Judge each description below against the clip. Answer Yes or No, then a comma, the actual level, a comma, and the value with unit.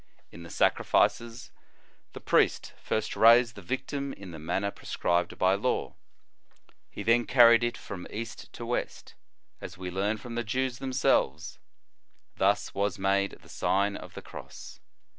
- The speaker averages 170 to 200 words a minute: No, average, 150 wpm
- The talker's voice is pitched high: No, low, 110 Hz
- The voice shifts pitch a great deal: No, average, 3.7 semitones